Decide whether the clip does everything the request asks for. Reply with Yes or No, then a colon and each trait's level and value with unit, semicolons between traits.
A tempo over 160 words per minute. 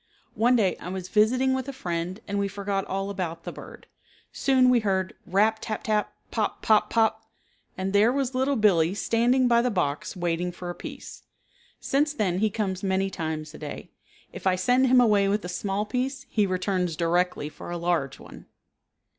Yes: average, 190 wpm